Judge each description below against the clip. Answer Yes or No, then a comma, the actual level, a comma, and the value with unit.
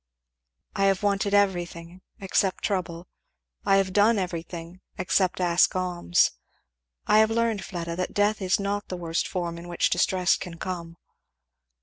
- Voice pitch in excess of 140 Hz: Yes, medium, 185 Hz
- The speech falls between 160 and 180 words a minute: No, average, 145 wpm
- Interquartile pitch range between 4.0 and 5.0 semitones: No, narrow, 2.4 semitones